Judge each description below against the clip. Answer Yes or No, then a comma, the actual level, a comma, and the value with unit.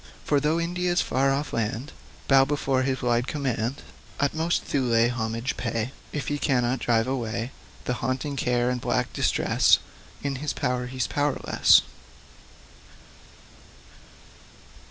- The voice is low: Yes, low, 130 Hz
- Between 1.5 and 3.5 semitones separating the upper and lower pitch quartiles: Yes, average, 2.9 semitones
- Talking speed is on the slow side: Yes, slow, 120 wpm